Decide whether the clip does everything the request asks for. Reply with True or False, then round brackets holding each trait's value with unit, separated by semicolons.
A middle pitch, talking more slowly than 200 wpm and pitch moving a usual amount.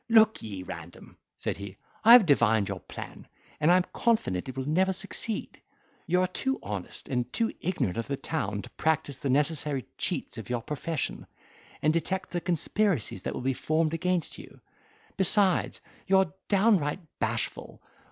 False (160 Hz; 165 wpm; 7.1 semitones)